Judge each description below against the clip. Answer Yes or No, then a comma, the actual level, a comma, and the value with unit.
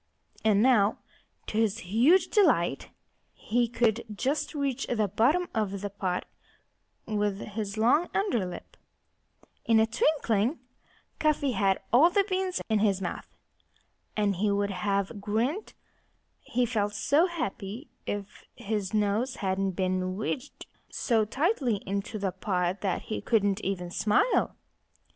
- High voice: Yes, high, 215 Hz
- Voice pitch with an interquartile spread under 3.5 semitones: No, average, 4.1 semitones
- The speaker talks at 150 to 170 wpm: No, slow, 135 wpm